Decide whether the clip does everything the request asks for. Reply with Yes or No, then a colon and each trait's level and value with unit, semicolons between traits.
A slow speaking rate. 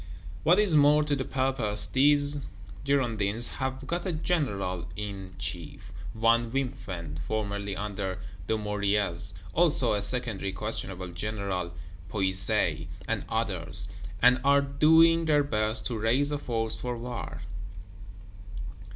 Yes: slow, 120 wpm